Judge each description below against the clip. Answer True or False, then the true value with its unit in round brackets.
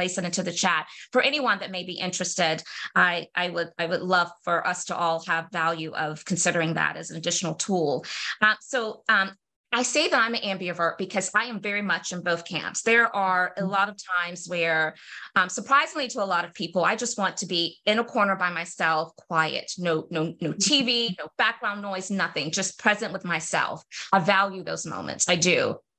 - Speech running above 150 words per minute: True (205 wpm)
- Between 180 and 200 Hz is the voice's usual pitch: True (185 Hz)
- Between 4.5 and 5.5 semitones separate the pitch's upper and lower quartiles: False (3.3 semitones)